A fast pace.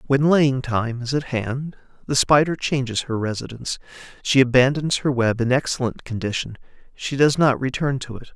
No: average, 170 wpm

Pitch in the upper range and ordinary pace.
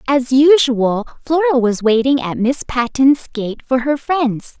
Yes: very high, 260 Hz; average, 155 wpm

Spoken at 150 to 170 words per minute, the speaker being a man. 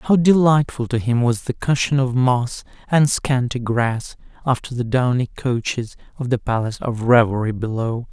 Yes: average, 165 wpm; male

